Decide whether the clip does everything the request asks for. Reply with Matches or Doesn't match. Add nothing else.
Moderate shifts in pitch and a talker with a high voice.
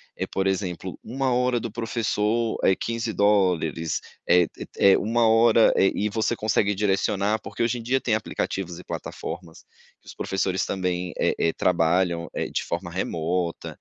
Doesn't match